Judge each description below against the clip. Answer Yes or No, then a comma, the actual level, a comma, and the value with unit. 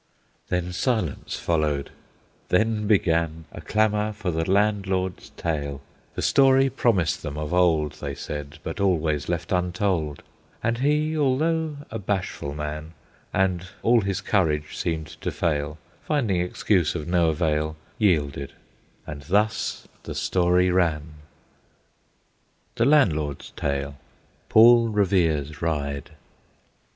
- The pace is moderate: No, slow, 120 wpm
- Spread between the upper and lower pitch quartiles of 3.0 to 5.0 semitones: No, wide, 5.5 semitones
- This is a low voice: Yes, very low, 90 Hz